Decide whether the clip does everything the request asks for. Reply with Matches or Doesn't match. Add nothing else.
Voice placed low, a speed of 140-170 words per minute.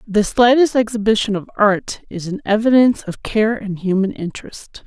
Doesn't match